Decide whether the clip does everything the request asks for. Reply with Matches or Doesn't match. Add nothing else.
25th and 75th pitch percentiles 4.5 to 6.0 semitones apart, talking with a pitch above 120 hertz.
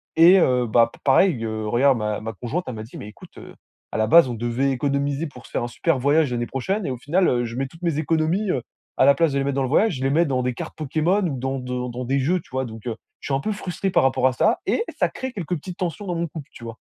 Matches